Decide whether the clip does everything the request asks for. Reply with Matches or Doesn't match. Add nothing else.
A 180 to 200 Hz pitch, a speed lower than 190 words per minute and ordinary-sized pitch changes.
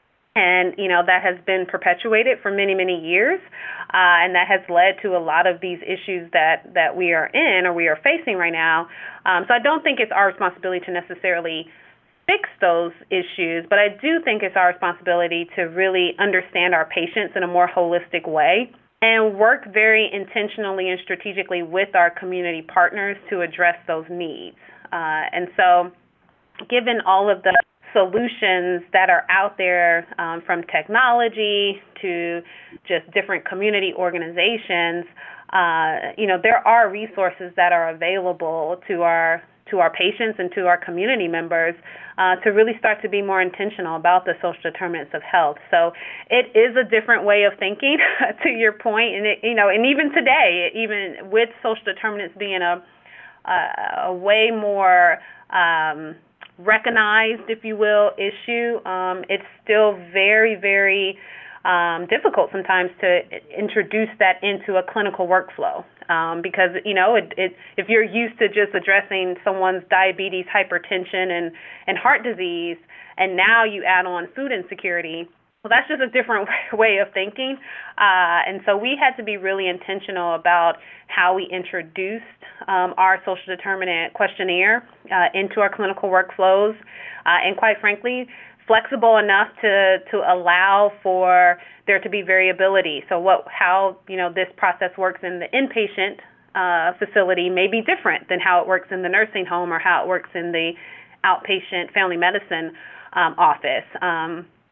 Matches